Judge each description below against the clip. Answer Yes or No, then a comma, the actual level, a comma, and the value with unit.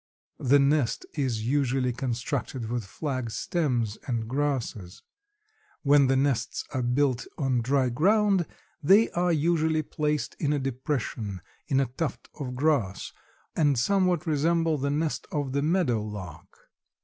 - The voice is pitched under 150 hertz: Yes, medium, 140 Hz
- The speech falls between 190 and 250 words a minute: No, slow, 135 wpm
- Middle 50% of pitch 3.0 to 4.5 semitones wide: Yes, average, 3.9 semitones